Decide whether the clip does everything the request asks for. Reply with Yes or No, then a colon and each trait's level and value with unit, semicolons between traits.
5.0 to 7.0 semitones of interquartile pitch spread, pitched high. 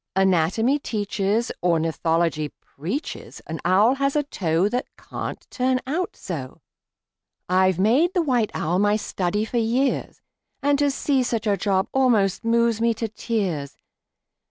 Yes: wide, 5.6 semitones; high, 215 Hz